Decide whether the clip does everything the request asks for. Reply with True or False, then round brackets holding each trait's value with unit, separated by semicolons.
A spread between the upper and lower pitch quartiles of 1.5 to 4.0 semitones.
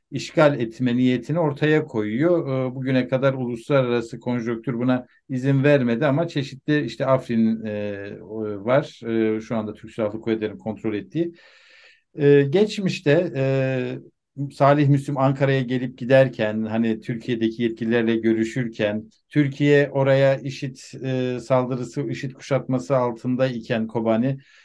True (3.5 semitones)